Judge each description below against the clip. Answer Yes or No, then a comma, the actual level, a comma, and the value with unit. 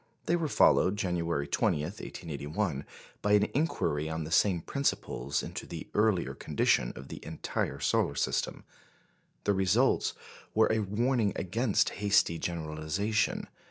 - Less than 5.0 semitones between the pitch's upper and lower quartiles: No, average, 5.3 semitones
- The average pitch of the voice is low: Yes, very low, 95 Hz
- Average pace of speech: No, slow, 130 wpm